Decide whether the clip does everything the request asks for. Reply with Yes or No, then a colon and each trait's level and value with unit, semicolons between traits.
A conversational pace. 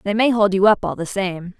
No: fast, 300 wpm